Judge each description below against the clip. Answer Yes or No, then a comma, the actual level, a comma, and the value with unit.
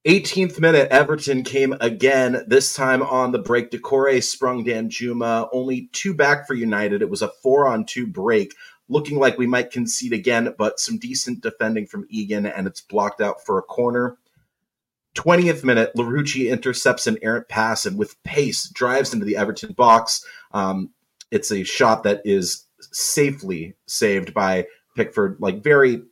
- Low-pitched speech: Yes, low, 125 Hz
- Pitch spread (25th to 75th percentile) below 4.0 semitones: Yes, average, 3.2 semitones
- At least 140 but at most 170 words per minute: Yes, average, 165 wpm